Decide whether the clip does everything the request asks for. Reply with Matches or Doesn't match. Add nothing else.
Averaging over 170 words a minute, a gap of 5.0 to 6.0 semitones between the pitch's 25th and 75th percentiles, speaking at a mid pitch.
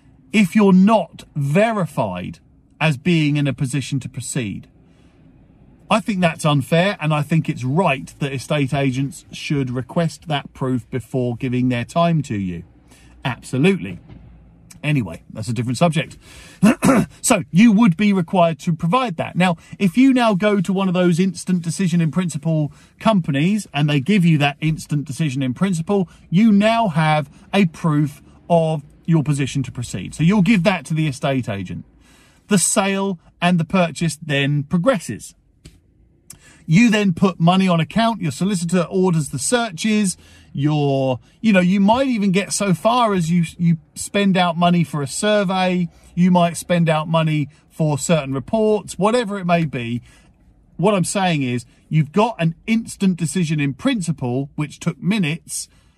Doesn't match